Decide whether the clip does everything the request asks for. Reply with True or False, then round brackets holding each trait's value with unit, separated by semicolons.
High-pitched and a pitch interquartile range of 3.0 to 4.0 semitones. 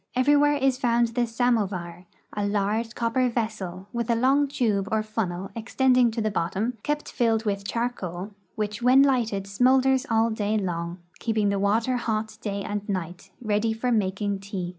True (220 Hz; 3.4 semitones)